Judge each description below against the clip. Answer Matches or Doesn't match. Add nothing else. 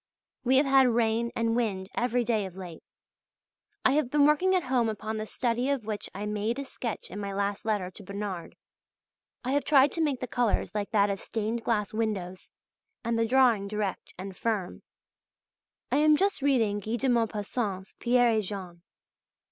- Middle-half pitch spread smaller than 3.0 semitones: Doesn't match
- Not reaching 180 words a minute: Doesn't match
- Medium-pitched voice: Doesn't match